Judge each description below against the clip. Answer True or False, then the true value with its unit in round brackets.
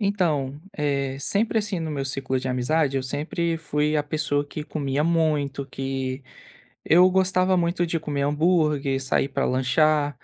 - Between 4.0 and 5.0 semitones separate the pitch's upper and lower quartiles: False (3.4 semitones)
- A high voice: False (150 Hz)